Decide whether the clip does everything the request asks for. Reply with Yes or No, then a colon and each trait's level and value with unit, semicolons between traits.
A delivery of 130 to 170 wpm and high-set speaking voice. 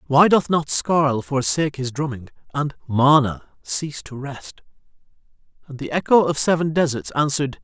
No: average, 165 wpm; medium, 140 Hz